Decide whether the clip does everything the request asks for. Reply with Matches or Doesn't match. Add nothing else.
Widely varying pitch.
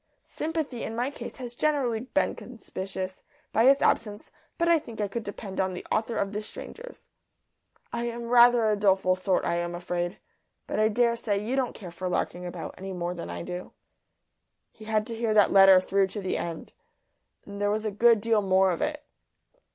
Doesn't match